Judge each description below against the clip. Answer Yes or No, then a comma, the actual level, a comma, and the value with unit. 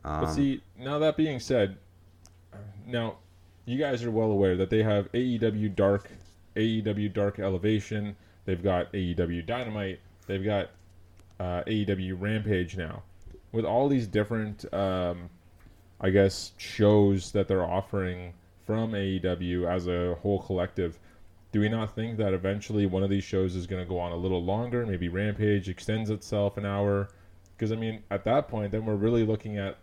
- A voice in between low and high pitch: No, low, 100 Hz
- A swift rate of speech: No, average, 165 wpm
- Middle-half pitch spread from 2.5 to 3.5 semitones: Yes, average, 2.8 semitones